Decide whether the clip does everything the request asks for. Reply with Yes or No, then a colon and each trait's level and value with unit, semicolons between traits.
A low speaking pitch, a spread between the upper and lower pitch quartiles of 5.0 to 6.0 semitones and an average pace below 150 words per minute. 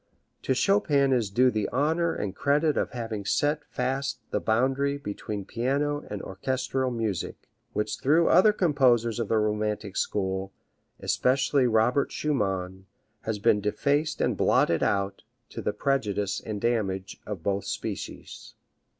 Yes: low, 120 Hz; average, 5.3 semitones; average, 140 wpm